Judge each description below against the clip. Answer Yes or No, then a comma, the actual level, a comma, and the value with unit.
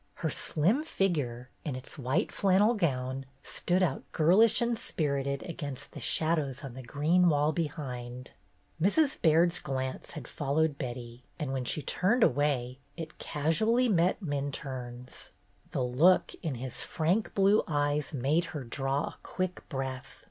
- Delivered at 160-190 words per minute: No, average, 150 wpm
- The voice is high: No, medium, 150 Hz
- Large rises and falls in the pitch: No, average, 5.0 semitones